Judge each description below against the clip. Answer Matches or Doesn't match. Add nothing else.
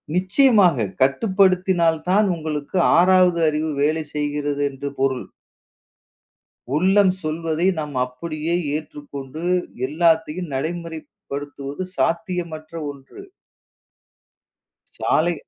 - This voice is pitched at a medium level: Matches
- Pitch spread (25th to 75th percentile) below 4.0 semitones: Matches